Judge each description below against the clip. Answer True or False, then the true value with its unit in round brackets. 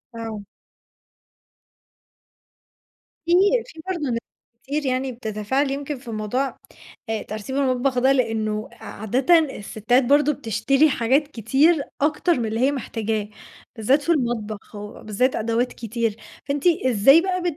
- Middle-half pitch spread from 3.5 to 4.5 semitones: True (4.2 semitones)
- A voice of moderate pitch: False (255 Hz)